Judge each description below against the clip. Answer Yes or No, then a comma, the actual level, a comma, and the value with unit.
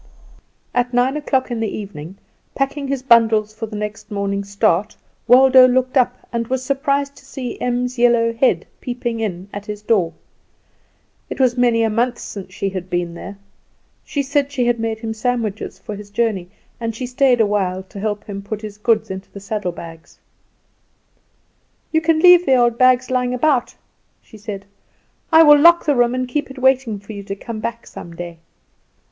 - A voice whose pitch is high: Yes, high, 230 Hz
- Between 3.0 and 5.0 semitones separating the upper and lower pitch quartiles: Yes, average, 3.9 semitones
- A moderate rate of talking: Yes, average, 185 wpm